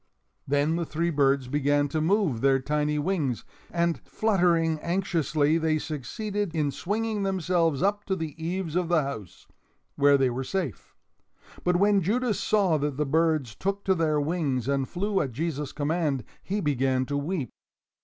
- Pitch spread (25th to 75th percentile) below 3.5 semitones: No, average, 4.4 semitones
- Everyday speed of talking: Yes, average, 165 wpm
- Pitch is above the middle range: No, medium, 160 Hz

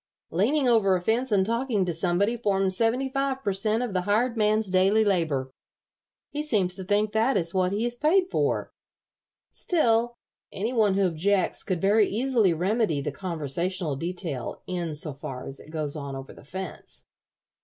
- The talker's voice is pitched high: Yes, high, 195 Hz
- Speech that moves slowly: No, average, 175 wpm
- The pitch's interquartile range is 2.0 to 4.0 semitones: No, average, 4.7 semitones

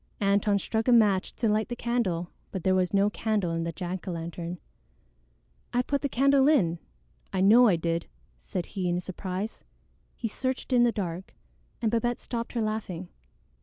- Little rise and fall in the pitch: No, average, 4.8 semitones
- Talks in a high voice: Yes, high, 200 Hz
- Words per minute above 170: Yes, average, 180 wpm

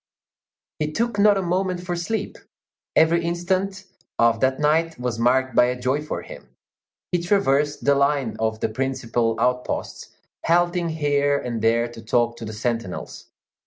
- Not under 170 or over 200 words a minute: No, average, 160 wpm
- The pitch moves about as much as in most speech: No, wide, 6.4 semitones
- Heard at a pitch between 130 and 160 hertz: Yes, medium, 140 Hz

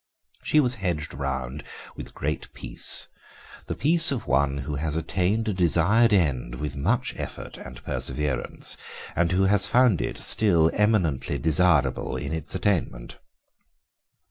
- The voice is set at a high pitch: No, very low, 85 Hz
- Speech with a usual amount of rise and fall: No, wide, 6.4 semitones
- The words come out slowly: No, average, 145 wpm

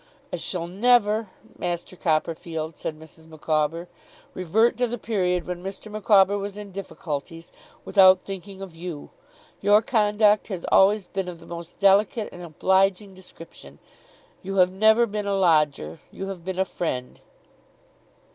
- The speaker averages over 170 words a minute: No, average, 145 wpm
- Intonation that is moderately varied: Yes, average, 3.3 semitones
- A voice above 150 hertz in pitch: Yes, high, 190 Hz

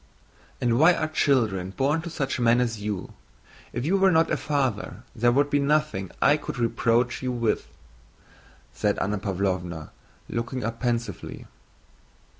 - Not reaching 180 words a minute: Yes, average, 150 wpm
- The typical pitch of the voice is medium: No, low, 120 Hz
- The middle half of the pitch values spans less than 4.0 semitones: No, average, 5.3 semitones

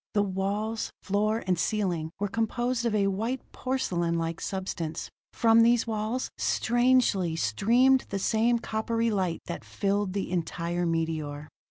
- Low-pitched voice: No, high, 205 Hz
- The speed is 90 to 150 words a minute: Yes, slow, 135 wpm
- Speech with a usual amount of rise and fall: Yes, average, 4.9 semitones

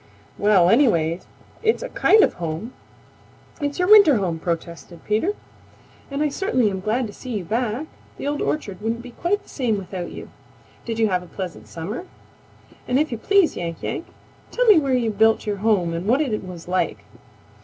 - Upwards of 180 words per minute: Yes, average, 190 wpm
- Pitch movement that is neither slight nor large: No, wide, 7.6 semitones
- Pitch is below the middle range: No, high, 220 Hz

